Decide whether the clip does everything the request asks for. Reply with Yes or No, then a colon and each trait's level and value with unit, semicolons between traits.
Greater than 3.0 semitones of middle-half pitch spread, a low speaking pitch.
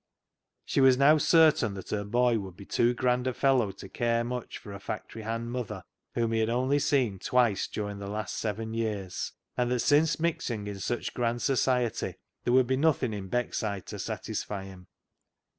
Yes: average, 3.6 semitones; low, 115 Hz